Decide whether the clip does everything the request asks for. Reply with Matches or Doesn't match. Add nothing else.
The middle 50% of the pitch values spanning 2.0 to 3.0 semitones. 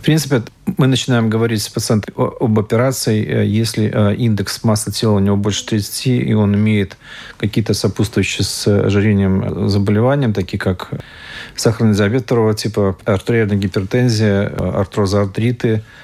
Matches